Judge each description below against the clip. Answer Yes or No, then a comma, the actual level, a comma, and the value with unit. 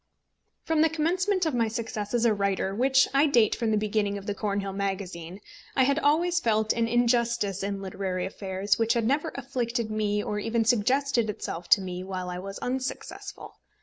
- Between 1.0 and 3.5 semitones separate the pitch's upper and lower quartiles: No, average, 4.4 semitones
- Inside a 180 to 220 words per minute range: Yes, average, 185 wpm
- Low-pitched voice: No, high, 220 Hz